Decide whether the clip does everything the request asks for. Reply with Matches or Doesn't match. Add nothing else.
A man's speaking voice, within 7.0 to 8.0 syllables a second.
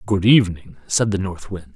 Doesn't match